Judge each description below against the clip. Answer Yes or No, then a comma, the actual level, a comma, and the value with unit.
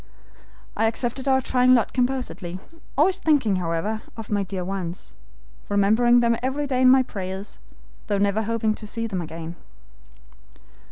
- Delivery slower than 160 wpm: Yes, average, 150 wpm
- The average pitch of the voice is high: Yes, high, 220 Hz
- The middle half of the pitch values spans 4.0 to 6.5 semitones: Yes, average, 4.7 semitones